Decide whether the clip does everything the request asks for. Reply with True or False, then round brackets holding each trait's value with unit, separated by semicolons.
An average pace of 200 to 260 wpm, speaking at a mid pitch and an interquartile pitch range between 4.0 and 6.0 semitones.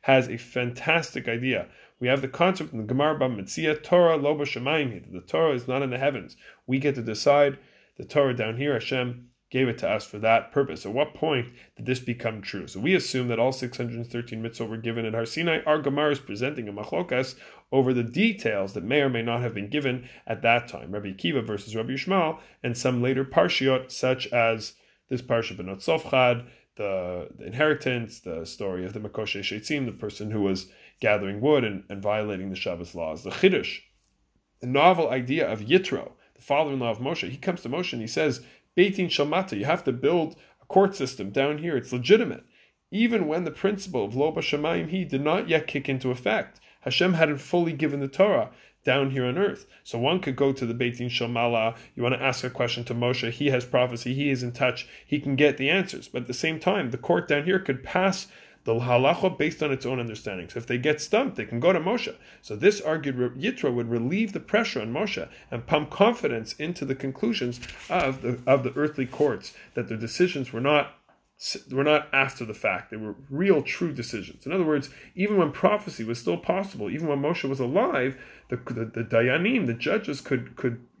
False (205 wpm; 130 Hz; 4.3 semitones)